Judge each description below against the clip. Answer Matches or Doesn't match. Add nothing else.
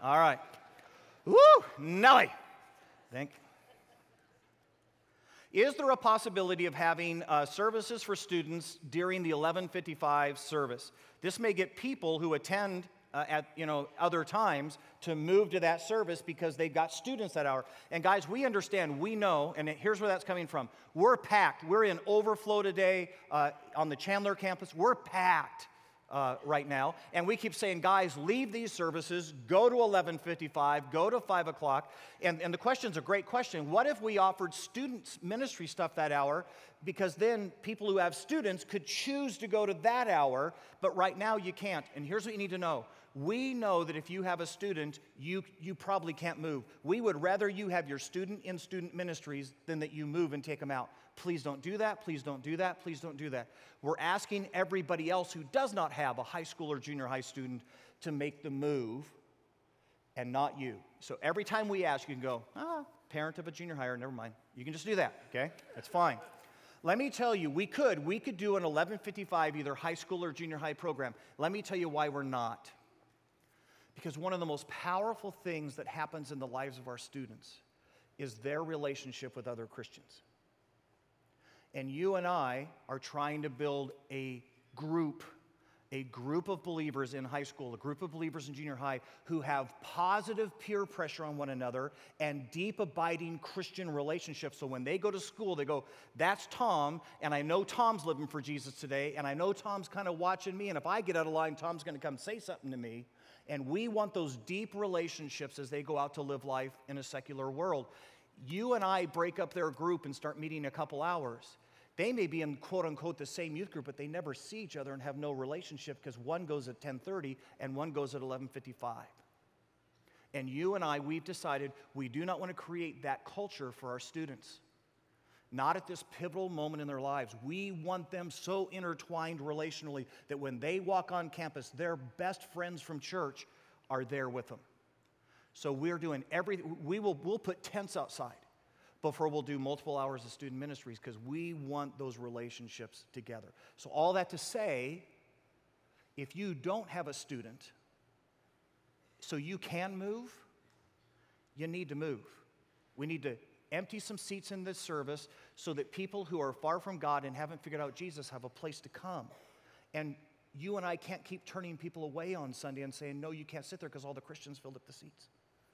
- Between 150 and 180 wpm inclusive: Doesn't match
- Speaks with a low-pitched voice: Doesn't match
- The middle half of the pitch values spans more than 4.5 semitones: Matches